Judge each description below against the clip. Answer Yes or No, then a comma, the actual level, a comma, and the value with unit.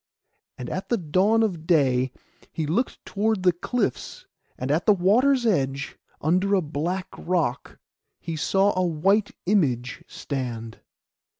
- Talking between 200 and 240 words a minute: No, slow, 135 wpm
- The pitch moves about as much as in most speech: No, wide, 5.9 semitones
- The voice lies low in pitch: No, medium, 175 Hz